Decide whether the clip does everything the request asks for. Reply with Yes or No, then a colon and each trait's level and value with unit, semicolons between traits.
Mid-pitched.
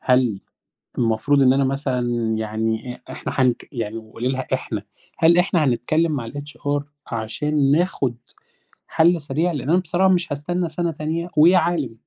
Yes: medium, 145 Hz